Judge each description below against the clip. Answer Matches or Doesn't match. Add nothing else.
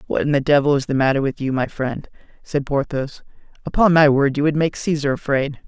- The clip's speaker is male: Matches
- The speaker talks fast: Matches